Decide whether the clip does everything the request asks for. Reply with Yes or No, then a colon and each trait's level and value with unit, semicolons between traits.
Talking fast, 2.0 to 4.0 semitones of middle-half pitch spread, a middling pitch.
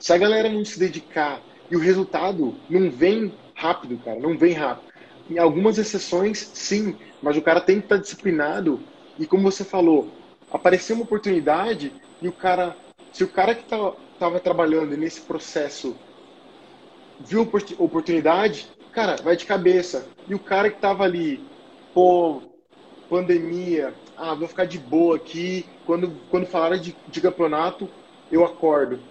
No: average, 155 wpm; average, 3.4 semitones; medium, 180 Hz